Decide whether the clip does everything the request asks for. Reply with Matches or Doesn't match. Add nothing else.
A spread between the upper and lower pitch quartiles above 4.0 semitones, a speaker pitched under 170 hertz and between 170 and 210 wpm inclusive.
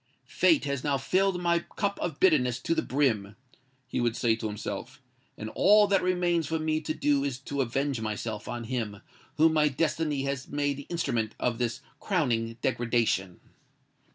Matches